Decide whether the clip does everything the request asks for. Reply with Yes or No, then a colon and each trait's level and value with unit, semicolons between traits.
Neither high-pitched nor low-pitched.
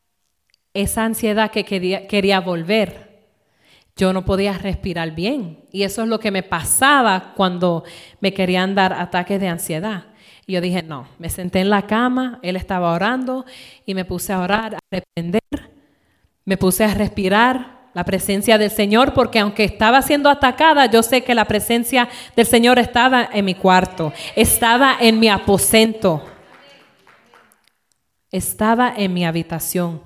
No: high, 200 Hz